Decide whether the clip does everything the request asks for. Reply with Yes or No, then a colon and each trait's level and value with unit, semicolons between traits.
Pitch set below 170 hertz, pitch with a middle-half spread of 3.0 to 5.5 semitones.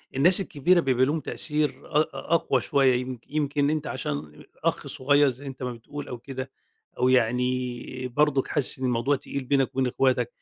No: low, 135 Hz; narrow, 2.6 semitones